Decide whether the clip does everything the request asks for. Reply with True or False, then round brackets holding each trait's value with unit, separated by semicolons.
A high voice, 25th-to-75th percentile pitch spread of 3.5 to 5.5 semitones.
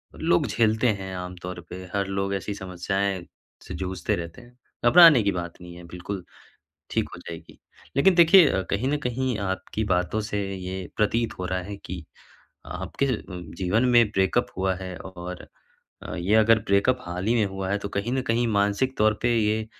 False (100 Hz; 3.9 semitones)